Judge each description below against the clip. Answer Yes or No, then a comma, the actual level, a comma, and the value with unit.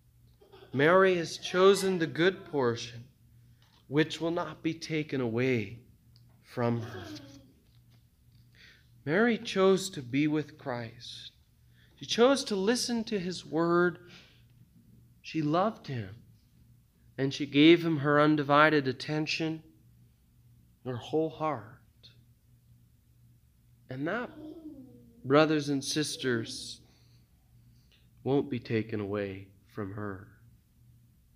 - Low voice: Yes, low, 130 Hz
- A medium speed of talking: No, slow, 100 wpm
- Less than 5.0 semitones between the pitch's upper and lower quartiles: No, average, 5.3 semitones